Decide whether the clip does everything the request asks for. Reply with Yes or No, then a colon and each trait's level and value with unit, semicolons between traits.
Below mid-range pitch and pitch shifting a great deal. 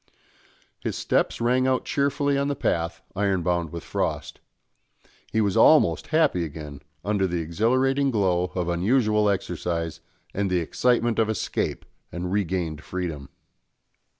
Yes: very low, 95 Hz; wide, 6.0 semitones